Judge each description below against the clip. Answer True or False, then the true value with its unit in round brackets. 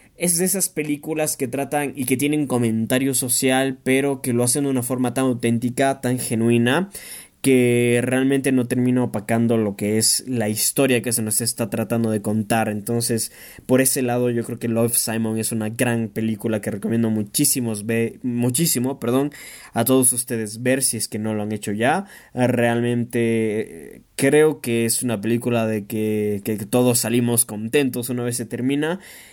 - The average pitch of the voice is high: False (120 Hz)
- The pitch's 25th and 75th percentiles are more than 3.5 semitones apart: False (2.6 semitones)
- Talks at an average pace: True (175 wpm)